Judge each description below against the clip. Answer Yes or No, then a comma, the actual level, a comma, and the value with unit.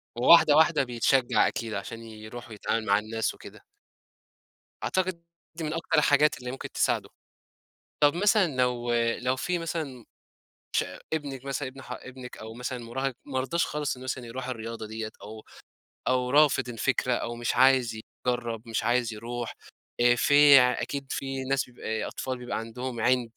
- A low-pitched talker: Yes, low, 125 Hz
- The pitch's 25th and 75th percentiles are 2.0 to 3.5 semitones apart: Yes, average, 2.9 semitones